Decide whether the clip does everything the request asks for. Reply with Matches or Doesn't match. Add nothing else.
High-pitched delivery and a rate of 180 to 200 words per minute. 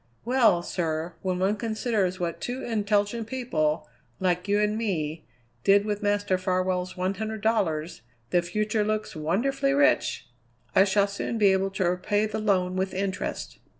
Doesn't match